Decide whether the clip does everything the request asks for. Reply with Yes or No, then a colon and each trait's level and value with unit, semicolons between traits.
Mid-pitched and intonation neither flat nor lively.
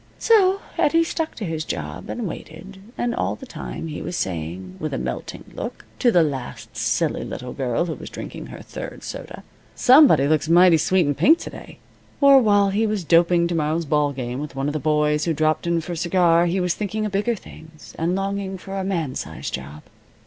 Yes: medium, 170 Hz; average, 5.0 semitones